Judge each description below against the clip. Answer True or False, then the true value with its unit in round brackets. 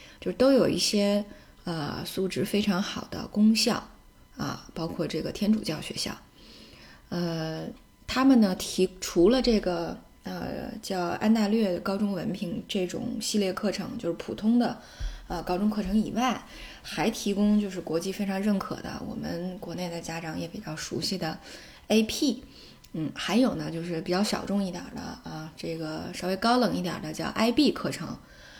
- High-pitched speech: True (205 Hz)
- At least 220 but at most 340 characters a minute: True (245 characters per minute)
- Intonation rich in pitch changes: False (3.8 semitones)